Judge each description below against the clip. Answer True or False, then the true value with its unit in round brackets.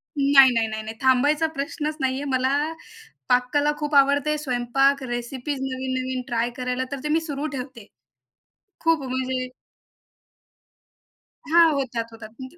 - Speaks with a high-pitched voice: True (265 Hz)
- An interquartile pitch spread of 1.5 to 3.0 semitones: True (2.4 semitones)